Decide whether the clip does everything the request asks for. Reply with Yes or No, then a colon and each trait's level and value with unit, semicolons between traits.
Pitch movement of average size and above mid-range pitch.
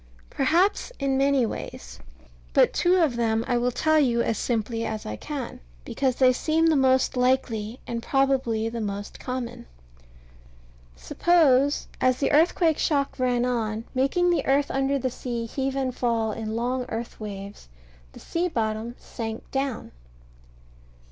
Yes: average, 3.3 semitones; very high, 255 Hz